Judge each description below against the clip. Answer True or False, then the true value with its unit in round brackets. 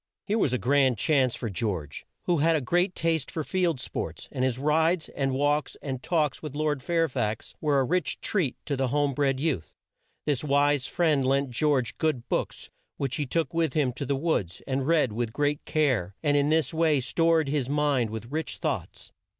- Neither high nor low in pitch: True (145 Hz)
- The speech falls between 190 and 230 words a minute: True (200 wpm)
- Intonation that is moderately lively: True (3.4 semitones)